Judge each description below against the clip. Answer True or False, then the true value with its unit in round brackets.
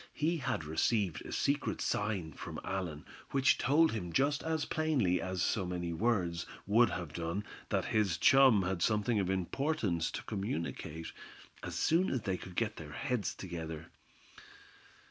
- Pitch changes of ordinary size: False (6.7 semitones)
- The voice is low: True (95 Hz)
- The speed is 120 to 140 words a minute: False (155 wpm)